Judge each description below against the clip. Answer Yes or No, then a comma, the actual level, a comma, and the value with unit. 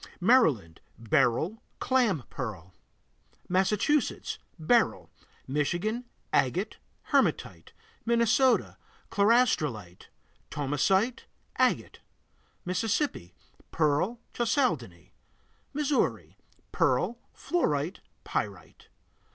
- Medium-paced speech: No, slow, 60 wpm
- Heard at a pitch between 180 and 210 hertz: Yes, medium, 185 Hz